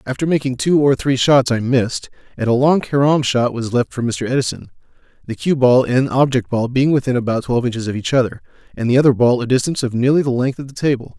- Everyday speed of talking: No, fast, 240 wpm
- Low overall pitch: Yes, low, 130 Hz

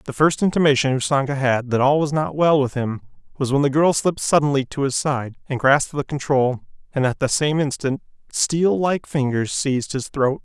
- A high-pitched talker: No, medium, 140 Hz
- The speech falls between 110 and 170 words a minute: No, fast, 205 wpm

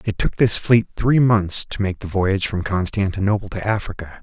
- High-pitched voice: No, low, 100 Hz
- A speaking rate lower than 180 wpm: No, average, 200 wpm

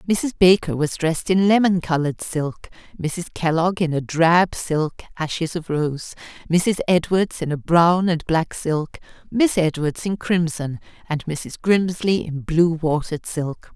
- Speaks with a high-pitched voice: No, medium, 165 Hz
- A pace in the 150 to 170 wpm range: Yes, average, 155 wpm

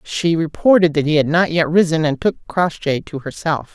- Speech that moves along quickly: Yes, fast, 210 wpm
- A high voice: No, medium, 160 Hz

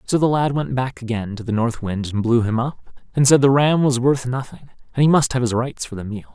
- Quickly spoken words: Yes, fast, 285 wpm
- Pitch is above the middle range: No, low, 125 Hz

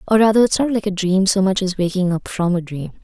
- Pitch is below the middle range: No, high, 190 Hz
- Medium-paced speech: No, fast, 295 wpm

